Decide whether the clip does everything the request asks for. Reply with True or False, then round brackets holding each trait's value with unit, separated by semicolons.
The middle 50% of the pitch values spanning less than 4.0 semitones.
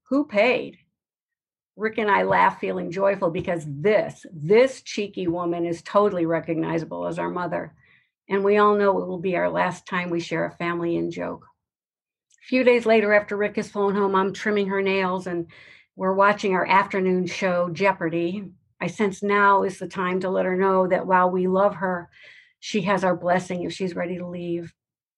True (2.6 semitones)